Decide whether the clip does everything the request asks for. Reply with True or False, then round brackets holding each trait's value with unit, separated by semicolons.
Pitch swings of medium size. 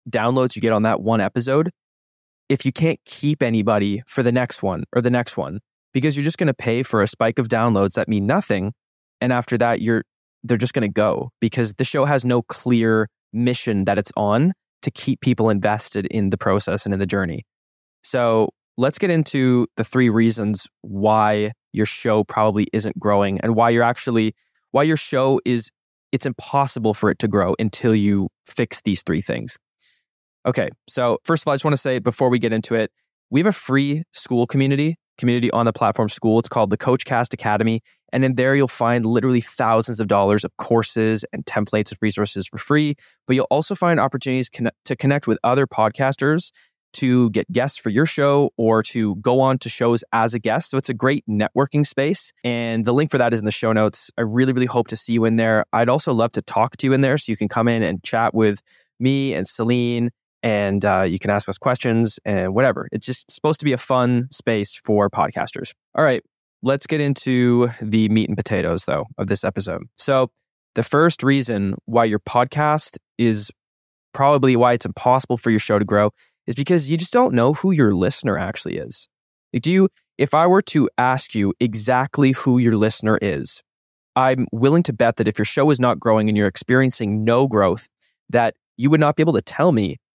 True (3.6 semitones)